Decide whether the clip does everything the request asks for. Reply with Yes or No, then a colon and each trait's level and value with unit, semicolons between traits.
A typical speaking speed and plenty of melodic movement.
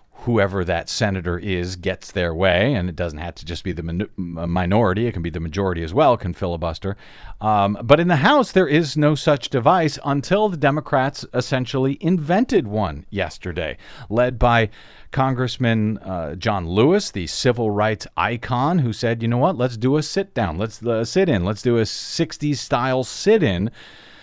Yes: average, 180 wpm; wide, 7.0 semitones